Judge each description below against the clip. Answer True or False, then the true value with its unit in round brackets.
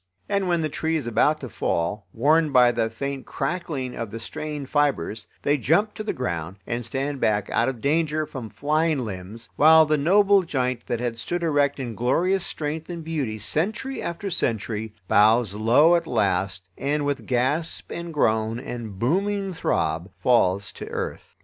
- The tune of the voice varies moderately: False (6.1 semitones)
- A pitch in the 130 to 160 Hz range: True (135 Hz)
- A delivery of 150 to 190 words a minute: True (175 wpm)